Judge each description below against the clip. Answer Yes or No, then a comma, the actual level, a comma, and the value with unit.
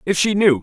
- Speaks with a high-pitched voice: No, medium, 175 Hz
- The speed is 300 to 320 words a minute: No, fast, 285 wpm